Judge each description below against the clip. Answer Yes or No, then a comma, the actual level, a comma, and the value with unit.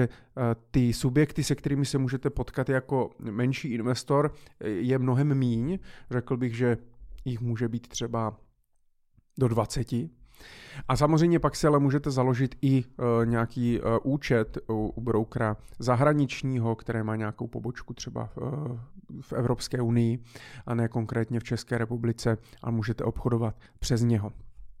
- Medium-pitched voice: No, low, 120 Hz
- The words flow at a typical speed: Yes, average, 130 wpm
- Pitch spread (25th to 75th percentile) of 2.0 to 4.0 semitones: Yes, narrow, 2.5 semitones